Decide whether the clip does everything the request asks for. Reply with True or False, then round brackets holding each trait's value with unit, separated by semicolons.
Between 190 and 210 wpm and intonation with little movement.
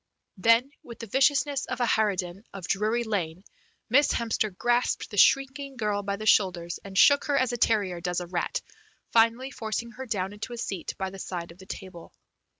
False (195 wpm; 4.3 semitones)